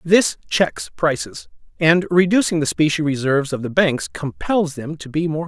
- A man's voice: Yes, male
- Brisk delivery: No, average, 185 wpm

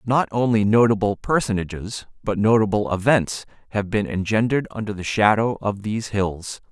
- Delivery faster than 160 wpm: No, average, 145 wpm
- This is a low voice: Yes, low, 105 Hz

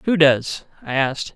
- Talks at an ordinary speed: Yes, average, 175 wpm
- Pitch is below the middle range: No, medium, 150 Hz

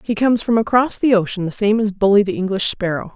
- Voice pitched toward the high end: Yes, high, 210 Hz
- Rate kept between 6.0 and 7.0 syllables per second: Yes, 6.2 syllables/s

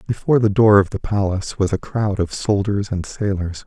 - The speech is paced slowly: No, fast, 215 wpm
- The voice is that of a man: Yes, male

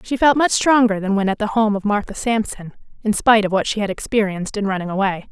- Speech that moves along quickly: Yes, fast, 250 wpm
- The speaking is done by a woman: Yes, female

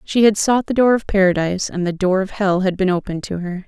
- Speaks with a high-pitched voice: Yes, high, 195 Hz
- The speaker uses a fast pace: Yes, fast, 275 wpm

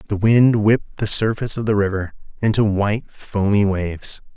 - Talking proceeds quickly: No, average, 165 wpm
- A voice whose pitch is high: No, low, 105 Hz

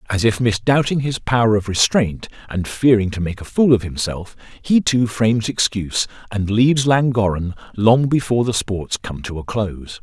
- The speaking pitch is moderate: No, low, 110 Hz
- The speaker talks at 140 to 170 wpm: No, average, 180 wpm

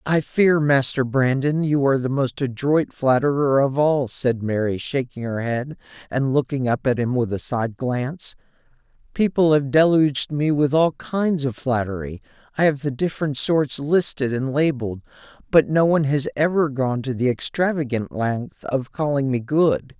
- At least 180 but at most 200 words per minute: No, average, 165 wpm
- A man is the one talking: Yes, male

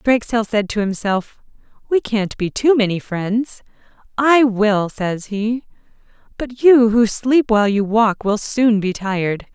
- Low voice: No, high, 220 Hz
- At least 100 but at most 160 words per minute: Yes, average, 155 wpm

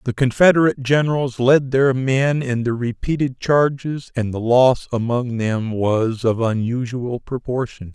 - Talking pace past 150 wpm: No, average, 145 wpm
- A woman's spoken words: No, male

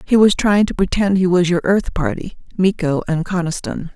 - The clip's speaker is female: Yes, female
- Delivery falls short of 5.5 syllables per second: Yes, 5.0 syllables/s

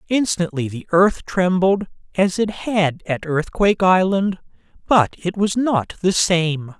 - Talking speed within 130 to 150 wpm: Yes, average, 140 wpm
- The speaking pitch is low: No, medium, 185 Hz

